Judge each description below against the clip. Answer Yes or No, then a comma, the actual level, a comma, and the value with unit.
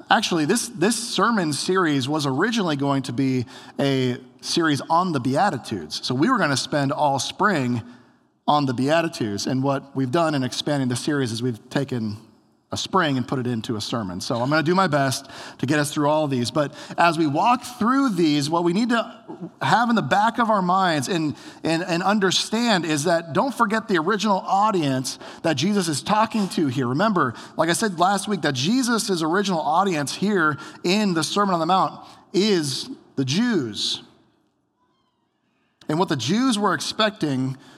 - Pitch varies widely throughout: Yes, wide, 6.3 semitones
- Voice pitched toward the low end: No, medium, 160 Hz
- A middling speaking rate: Yes, average, 190 wpm